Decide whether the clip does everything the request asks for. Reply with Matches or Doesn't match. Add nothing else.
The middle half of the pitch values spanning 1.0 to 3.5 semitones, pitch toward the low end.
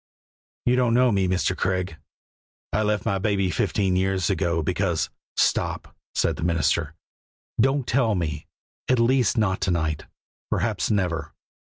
Doesn't match